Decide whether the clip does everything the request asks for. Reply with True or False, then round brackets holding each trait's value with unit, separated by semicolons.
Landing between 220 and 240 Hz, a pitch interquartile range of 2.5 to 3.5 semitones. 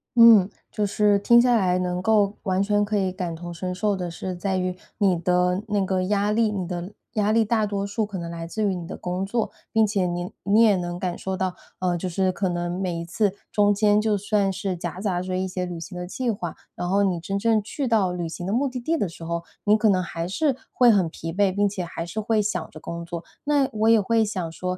False (190 Hz; 2.8 semitones)